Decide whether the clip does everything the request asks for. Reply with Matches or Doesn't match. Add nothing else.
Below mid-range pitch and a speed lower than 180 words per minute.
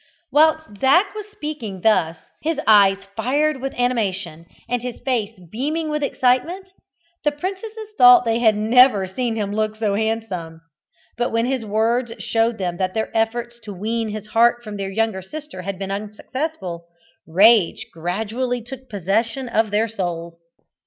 Doesn't match